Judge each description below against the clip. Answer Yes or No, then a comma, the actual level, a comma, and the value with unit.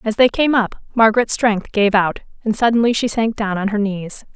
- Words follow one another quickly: Yes, fast, 220 wpm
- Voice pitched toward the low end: No, high, 215 Hz